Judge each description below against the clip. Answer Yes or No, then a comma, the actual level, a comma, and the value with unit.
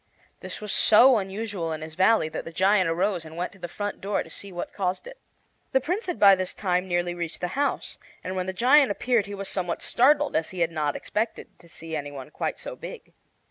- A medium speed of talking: No, fast, 235 wpm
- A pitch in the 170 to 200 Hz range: Yes, high, 190 Hz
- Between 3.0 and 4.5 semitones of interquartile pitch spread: Yes, average, 3.8 semitones